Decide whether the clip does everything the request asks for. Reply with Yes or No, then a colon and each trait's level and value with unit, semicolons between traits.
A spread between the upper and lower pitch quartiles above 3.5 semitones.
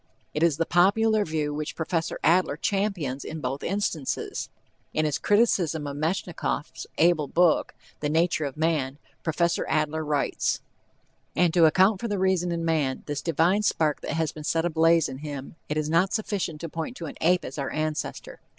No: average, 2.8 semitones